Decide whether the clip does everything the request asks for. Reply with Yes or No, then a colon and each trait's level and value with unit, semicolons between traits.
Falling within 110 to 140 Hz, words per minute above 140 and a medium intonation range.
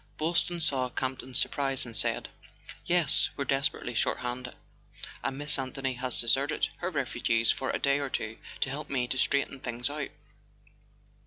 No: low, 135 Hz; average, 160 wpm; narrow, 2.2 semitones